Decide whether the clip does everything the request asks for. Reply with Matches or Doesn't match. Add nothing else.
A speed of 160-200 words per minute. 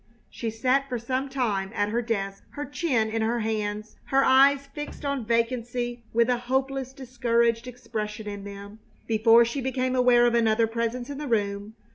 Matches